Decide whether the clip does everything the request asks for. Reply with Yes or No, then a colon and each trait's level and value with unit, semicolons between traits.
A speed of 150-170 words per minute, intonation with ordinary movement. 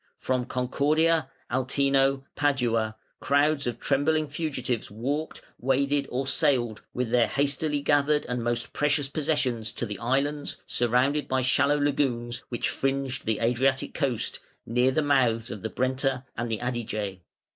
No: slow, 135 wpm; average, 3.0 semitones